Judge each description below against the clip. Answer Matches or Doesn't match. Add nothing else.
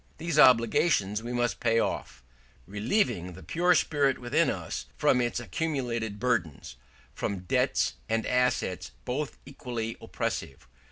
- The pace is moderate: Doesn't match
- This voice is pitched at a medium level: Doesn't match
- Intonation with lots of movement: Doesn't match